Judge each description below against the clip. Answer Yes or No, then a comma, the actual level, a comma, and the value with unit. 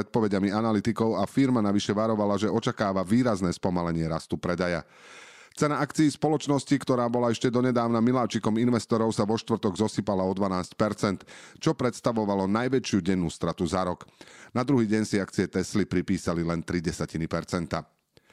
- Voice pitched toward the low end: Yes, low, 110 Hz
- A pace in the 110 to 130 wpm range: No, average, 145 wpm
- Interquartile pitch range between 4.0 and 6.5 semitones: Yes, average, 4.3 semitones